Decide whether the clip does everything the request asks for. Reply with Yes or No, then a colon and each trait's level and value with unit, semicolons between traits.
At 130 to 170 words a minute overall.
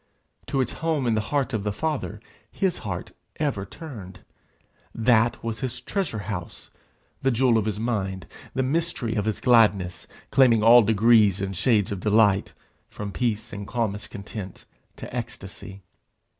Yes: average, 155 wpm